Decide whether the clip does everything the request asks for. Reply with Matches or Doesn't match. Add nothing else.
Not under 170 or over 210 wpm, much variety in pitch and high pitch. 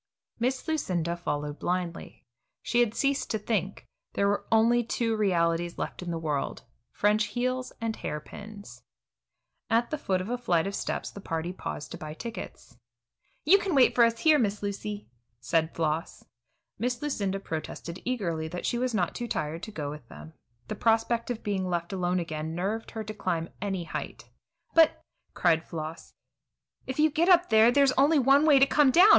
Matches